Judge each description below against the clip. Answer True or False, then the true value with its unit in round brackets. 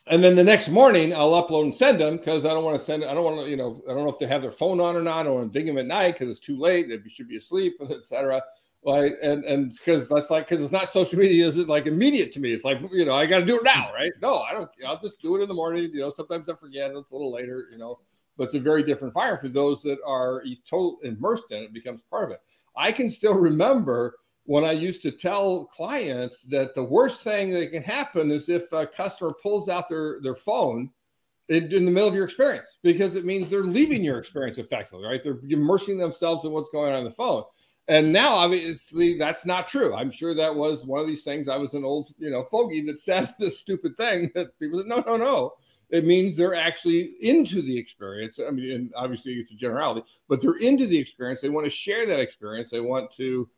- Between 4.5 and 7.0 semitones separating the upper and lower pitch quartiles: True (5.5 semitones)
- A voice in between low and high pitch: True (160 Hz)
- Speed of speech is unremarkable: False (260 wpm)